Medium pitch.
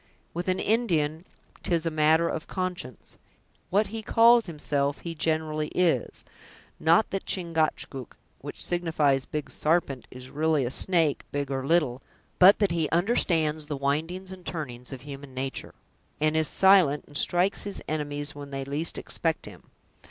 Yes: medium, 155 Hz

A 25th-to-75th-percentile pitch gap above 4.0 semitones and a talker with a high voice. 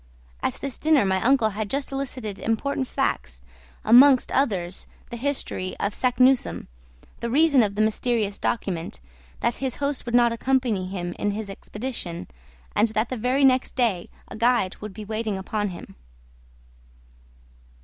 Yes: average, 4.4 semitones; high, 230 Hz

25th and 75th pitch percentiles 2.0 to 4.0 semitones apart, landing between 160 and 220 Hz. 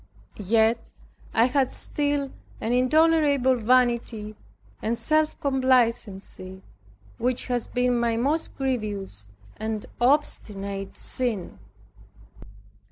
No: average, 3.4 semitones; high, 245 Hz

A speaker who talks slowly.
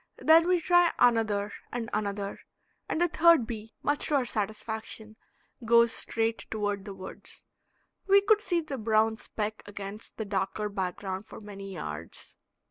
No: average, 150 wpm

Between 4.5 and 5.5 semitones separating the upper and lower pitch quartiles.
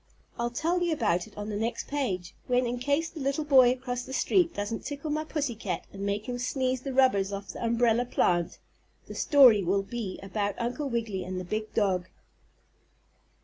Yes: average, 4.9 semitones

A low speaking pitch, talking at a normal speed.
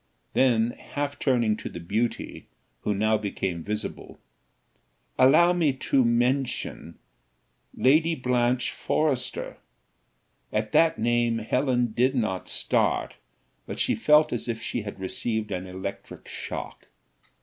No: low, 120 Hz; slow, 120 wpm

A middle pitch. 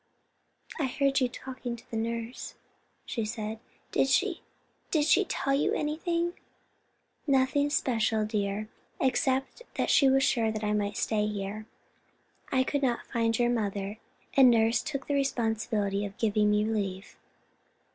No: high, 235 Hz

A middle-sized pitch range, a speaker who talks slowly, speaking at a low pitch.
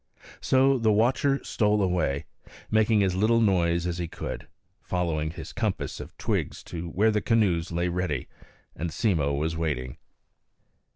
No: average, 4.8 semitones; average, 150 wpm; very low, 90 Hz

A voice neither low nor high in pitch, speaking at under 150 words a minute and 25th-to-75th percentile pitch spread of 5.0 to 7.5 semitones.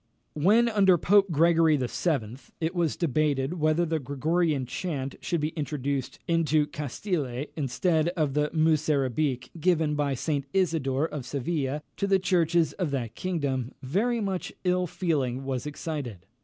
No: medium, 155 Hz; average, 140 wpm; average, 3.9 semitones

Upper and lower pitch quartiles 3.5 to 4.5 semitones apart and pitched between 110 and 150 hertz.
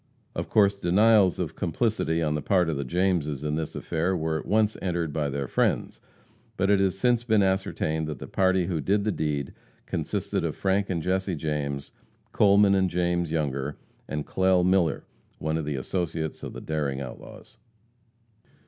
No: average, 4.1 semitones; very low, 85 Hz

